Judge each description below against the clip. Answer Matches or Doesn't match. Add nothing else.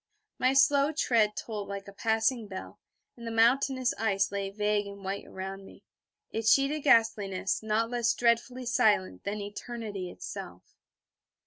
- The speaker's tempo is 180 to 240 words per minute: Doesn't match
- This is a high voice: Matches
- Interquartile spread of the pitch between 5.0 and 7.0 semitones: Doesn't match